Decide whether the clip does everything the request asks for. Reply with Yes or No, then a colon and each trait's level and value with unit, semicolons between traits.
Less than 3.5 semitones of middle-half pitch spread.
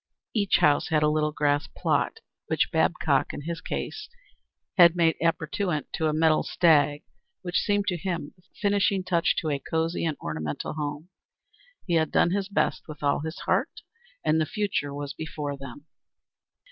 Yes: average, 3.1 semitones